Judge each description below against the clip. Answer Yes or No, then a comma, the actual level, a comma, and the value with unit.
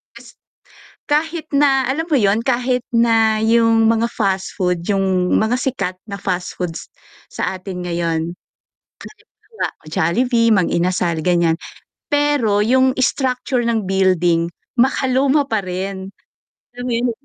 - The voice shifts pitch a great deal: Yes, wide, 5.7 semitones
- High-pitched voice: Yes, high, 220 Hz